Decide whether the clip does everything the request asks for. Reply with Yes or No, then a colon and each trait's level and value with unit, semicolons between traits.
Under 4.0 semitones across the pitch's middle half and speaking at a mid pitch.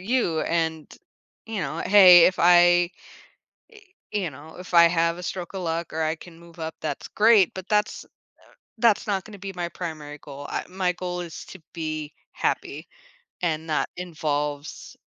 Yes: narrow, 2.5 semitones; medium, 170 Hz